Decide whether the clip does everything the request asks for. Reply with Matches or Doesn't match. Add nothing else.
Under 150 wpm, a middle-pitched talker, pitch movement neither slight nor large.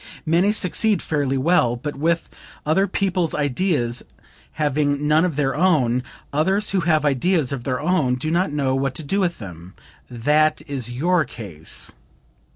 Doesn't match